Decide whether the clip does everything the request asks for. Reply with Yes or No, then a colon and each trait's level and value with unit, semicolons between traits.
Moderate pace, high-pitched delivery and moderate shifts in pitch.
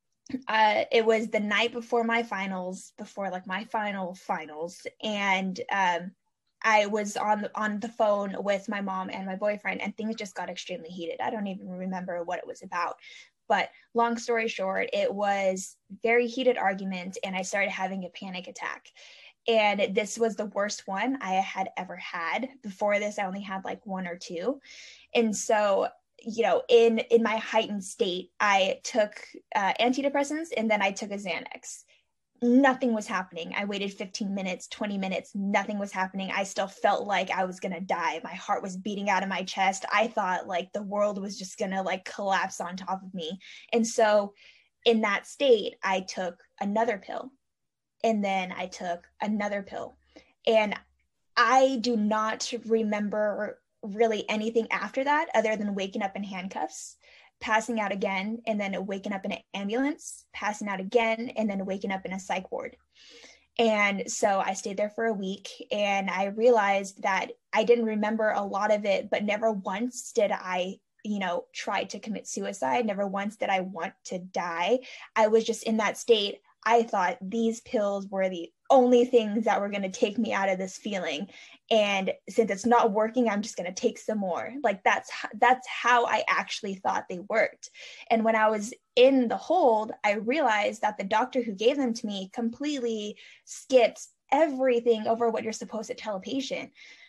Yes: average, 185 wpm; high, 210 Hz; average, 3.2 semitones